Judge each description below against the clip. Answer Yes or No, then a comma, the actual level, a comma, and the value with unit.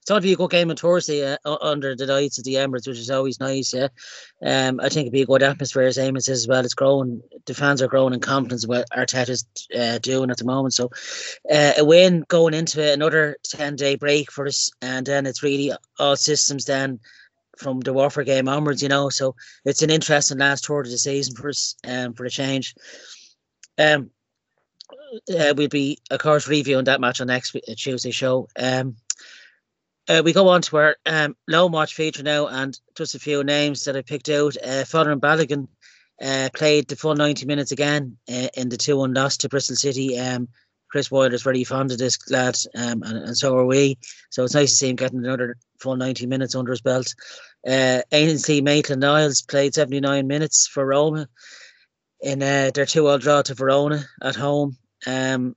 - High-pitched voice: No, low, 135 Hz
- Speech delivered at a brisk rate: Yes, fast, 210 wpm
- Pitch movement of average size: No, narrow, 2.1 semitones